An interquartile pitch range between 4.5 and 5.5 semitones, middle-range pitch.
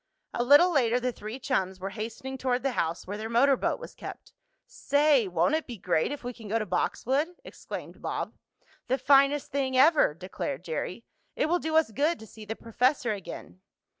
No: average, 5.2 semitones; high, 245 Hz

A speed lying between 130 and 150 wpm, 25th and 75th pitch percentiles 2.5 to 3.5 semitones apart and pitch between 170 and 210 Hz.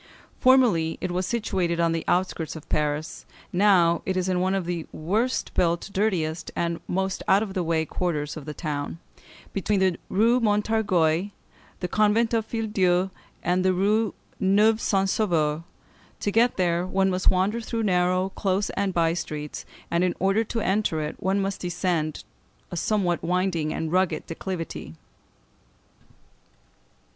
No: average, 160 wpm; average, 3.1 semitones; medium, 185 Hz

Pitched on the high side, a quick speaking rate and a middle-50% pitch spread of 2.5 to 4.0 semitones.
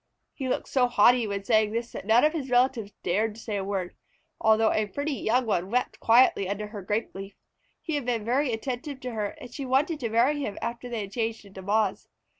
Yes: high, 225 Hz; fast, 230 wpm; average, 3.4 semitones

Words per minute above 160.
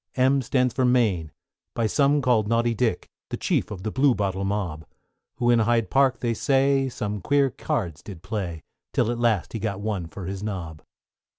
Yes: average, 185 wpm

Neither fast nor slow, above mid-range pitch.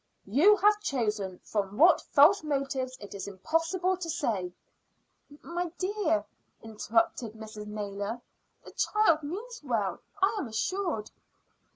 No: slow, 130 wpm; very high, 275 Hz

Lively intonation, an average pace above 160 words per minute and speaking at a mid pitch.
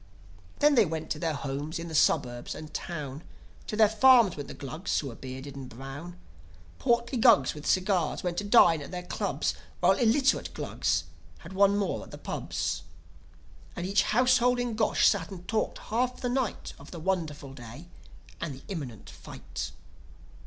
Yes: wide, 7.2 semitones; average, 175 wpm; medium, 175 Hz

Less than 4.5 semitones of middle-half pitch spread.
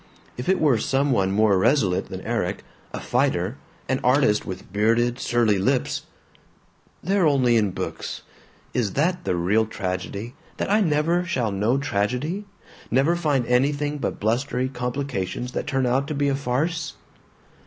No: average, 5.2 semitones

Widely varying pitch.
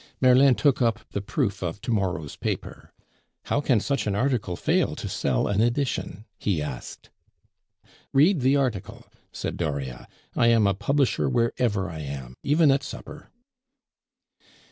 Yes: wide, 6.5 semitones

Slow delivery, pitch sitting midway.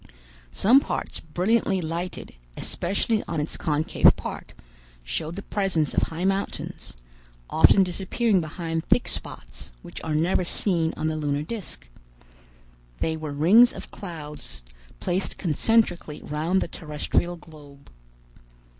Yes: slow, 125 wpm; medium, 165 Hz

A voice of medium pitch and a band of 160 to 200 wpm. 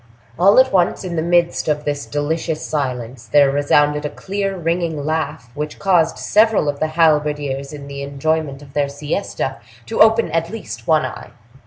Yes: medium, 150 Hz; average, 175 wpm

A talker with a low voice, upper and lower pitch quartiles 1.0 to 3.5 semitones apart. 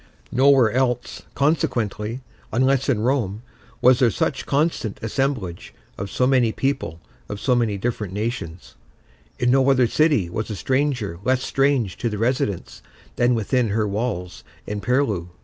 No: low, 120 Hz; average, 4.2 semitones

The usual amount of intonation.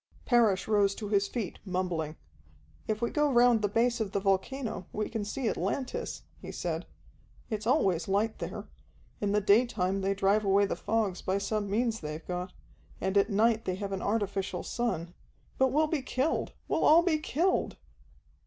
Yes: average, 3.5 semitones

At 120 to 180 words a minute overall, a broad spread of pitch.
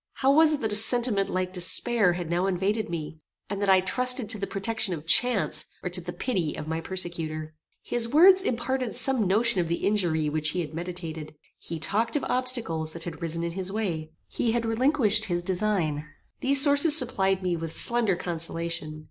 No: average, 195 wpm; wide, 5.9 semitones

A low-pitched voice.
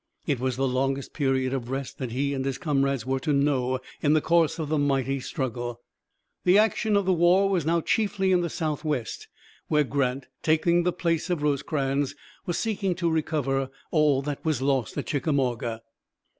No: medium, 145 Hz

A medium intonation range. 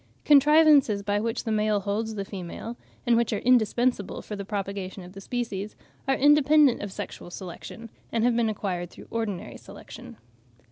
Yes: average, 3.5 semitones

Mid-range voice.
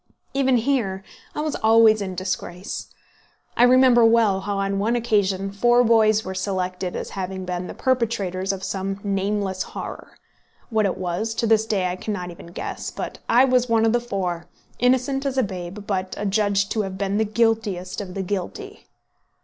No: high, 205 Hz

